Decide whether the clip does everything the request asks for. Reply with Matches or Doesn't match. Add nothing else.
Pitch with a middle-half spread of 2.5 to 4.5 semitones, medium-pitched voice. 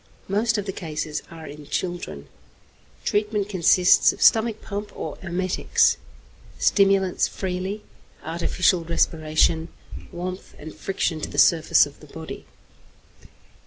Matches